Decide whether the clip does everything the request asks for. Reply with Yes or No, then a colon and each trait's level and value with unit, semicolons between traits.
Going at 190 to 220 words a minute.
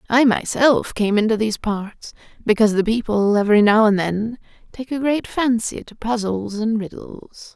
No: average, 165 wpm